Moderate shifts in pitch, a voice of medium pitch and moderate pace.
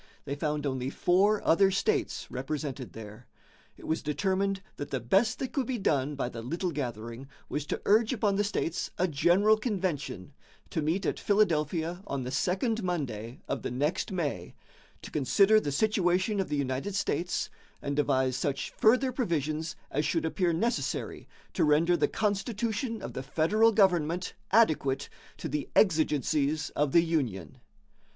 No: wide, 6.1 semitones; medium, 165 Hz; average, 160 wpm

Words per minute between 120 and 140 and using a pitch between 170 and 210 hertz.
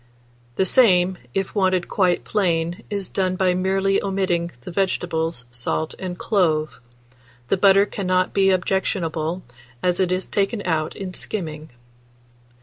Yes: slow, 135 wpm; medium, 185 Hz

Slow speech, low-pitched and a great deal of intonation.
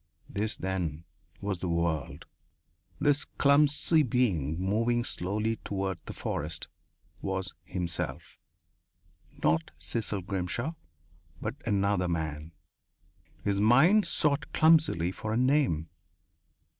Yes: slow, 100 wpm; low, 100 Hz; wide, 6.6 semitones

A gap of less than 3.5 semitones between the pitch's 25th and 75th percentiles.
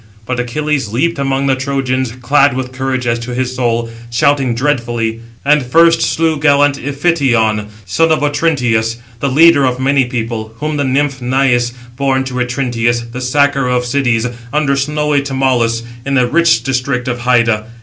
Yes: average, 2.8 semitones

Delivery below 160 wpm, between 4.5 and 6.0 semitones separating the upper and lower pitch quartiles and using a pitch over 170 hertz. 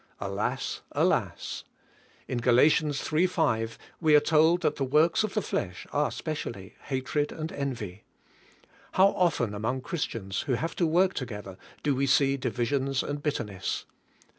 No: average, 145 wpm; average, 5.1 semitones; medium, 140 Hz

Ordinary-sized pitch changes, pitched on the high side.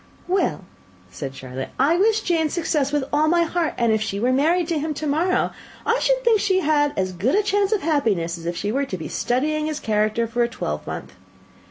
No: wide, 8.0 semitones; very high, 295 Hz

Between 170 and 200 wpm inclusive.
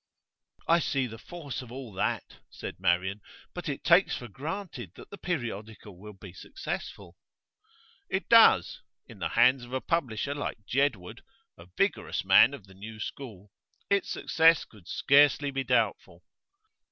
No: average, 155 wpm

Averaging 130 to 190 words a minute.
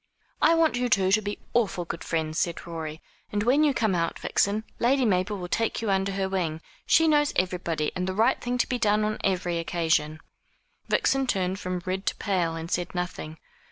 No: fast, 205 wpm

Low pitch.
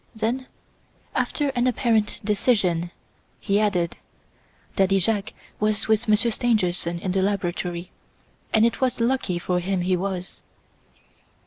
No: high, 205 Hz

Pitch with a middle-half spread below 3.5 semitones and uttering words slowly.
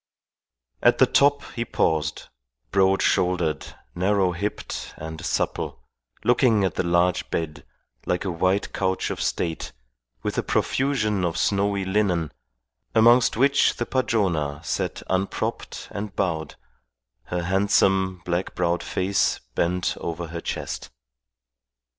Yes: average, 3.0 semitones; slow, 125 wpm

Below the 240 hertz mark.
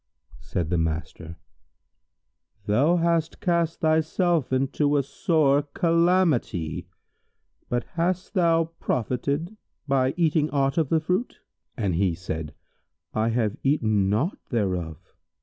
Yes: medium, 140 Hz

